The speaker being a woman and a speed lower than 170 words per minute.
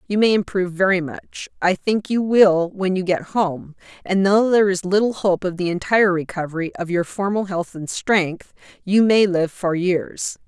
No: female; average, 195 wpm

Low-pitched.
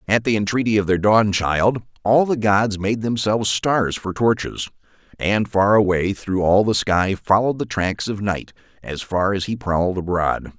Yes: low, 100 Hz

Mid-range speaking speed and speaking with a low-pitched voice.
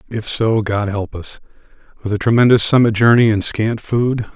Yes: average, 180 wpm; low, 110 Hz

